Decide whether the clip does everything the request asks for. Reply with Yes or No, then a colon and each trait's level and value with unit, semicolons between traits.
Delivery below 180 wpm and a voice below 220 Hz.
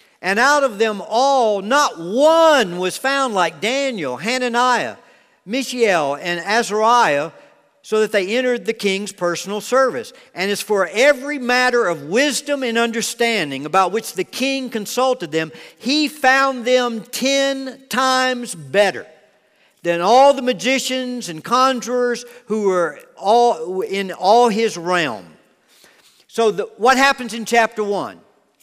No: slow, 135 wpm; high, 235 Hz